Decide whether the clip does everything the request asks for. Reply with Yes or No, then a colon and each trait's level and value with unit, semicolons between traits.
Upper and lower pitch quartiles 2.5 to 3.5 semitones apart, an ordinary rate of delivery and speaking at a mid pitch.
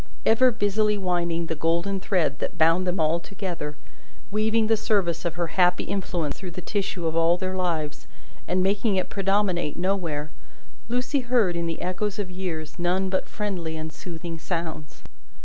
Yes: average, 3.1 semitones; average, 165 wpm; medium, 180 Hz